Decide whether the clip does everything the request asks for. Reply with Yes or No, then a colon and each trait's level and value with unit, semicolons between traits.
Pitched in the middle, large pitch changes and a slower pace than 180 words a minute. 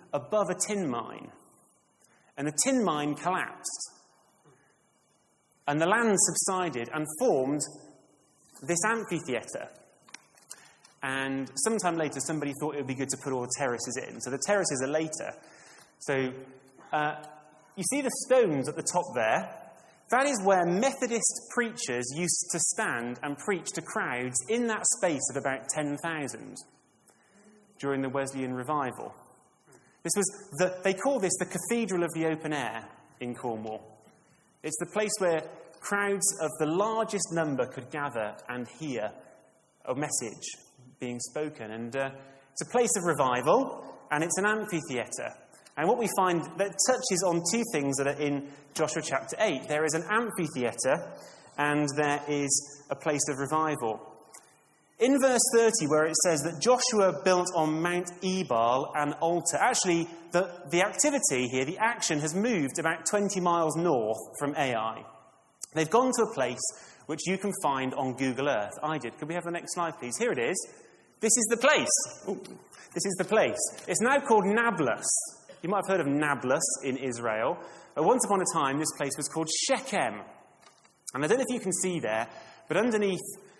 Yes: medium, 160 Hz; wide, 6.1 semitones; average, 165 wpm